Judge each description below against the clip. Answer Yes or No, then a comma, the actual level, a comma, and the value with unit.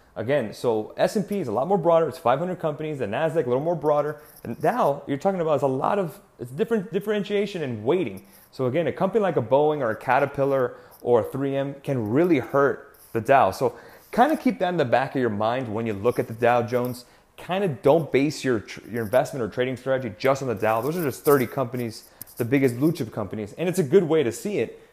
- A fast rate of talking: Yes, fast, 245 wpm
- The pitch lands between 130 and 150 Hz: Yes, medium, 140 Hz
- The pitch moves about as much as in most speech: No, wide, 5.9 semitones